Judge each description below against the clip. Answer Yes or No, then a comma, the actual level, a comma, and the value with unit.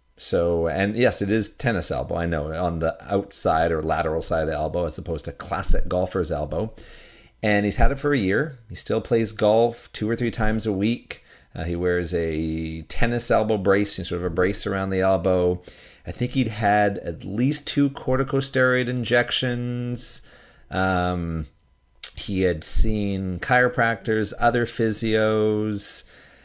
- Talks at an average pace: Yes, average, 160 wpm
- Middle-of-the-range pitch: No, low, 105 Hz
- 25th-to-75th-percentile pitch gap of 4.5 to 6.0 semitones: Yes, average, 4.8 semitones